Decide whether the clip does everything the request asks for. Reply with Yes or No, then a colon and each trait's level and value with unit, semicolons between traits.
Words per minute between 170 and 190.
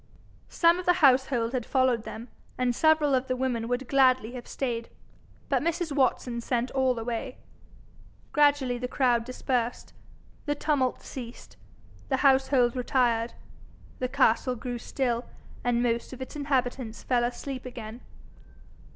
No: average, 140 wpm